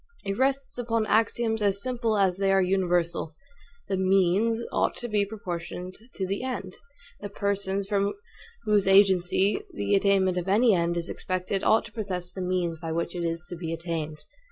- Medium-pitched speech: No, high, 195 Hz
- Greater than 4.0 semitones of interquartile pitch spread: No, average, 2.8 semitones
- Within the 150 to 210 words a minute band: Yes, average, 180 wpm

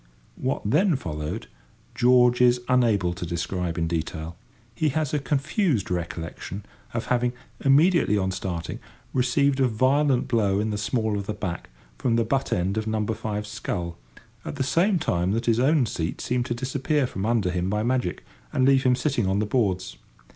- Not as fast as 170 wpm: No, average, 180 wpm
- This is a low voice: Yes, low, 115 Hz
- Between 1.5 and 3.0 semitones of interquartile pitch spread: No, wide, 5.6 semitones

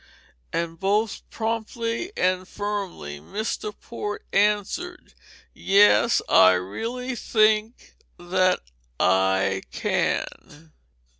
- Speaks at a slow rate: Yes, slow, 80 wpm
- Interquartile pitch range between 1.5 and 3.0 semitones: No, average, 5.3 semitones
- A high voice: Yes, high, 205 Hz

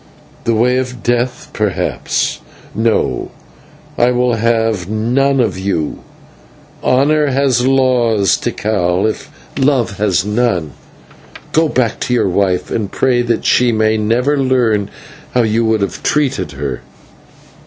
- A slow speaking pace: Yes, slow, 130 wpm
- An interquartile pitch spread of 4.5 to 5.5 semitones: No, average, 3.4 semitones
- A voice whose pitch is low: Yes, low, 115 Hz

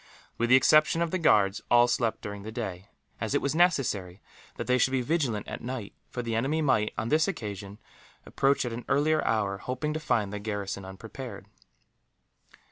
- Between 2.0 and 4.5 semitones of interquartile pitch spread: No, average, 5.3 semitones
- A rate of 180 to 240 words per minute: Yes, average, 190 wpm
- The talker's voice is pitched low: Yes, low, 120 Hz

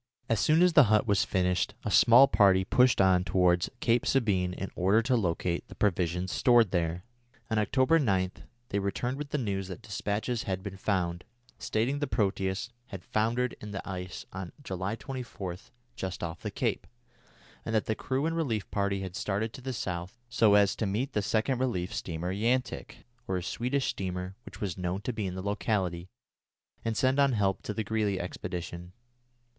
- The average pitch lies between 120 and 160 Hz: No, low, 100 Hz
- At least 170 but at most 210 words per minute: Yes, average, 185 wpm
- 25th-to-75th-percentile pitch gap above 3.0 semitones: Yes, average, 4.1 semitones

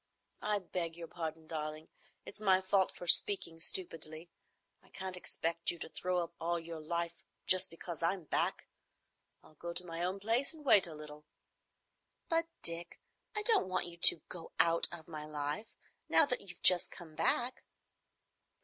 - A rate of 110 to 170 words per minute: Yes, average, 160 wpm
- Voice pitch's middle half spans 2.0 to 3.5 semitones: Yes, narrow, 2.5 semitones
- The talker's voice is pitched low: No, medium, 170 Hz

